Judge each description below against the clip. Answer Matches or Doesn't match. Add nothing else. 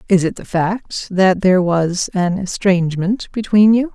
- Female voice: Matches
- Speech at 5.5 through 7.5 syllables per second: Doesn't match